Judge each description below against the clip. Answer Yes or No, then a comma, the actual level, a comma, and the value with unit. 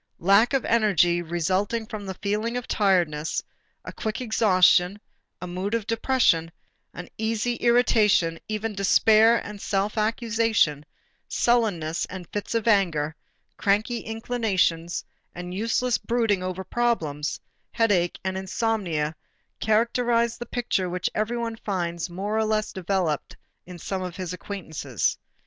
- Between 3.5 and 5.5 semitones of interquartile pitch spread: Yes, average, 4.1 semitones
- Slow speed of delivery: Yes, slow, 125 wpm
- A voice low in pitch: No, high, 200 Hz